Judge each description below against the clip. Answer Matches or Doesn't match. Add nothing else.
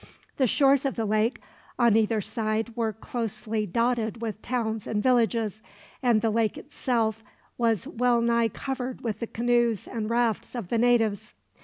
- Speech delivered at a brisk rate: Doesn't match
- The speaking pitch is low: Doesn't match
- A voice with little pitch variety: Matches